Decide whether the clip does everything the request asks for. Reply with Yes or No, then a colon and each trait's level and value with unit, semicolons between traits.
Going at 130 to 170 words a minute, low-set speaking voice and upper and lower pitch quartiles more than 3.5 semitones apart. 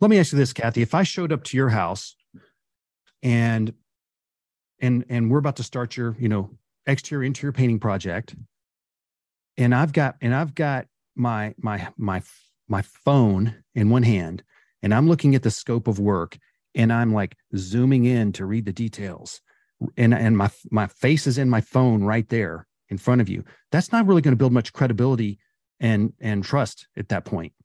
No: average, 190 wpm; low, 120 Hz; average, 3.9 semitones